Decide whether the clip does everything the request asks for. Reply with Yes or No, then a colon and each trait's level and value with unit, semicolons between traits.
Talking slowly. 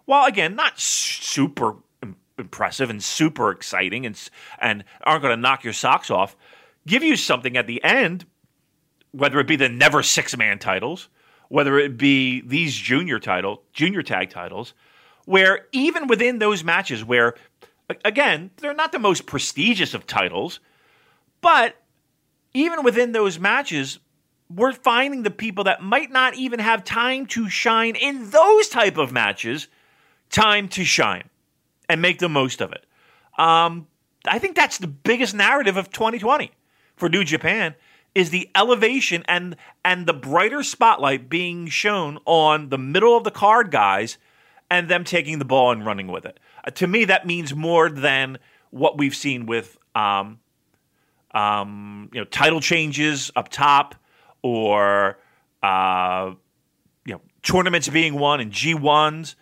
No: average, 155 wpm